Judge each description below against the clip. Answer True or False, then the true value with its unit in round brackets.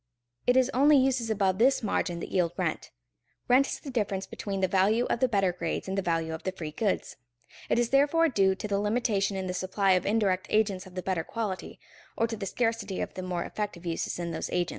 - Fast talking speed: True (230 wpm)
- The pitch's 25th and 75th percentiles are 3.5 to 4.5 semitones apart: True (3.8 semitones)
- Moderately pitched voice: False (195 Hz)